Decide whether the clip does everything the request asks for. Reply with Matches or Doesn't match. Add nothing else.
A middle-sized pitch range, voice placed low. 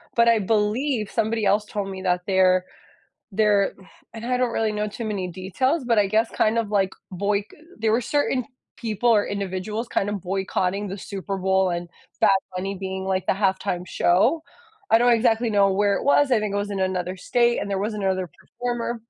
Doesn't match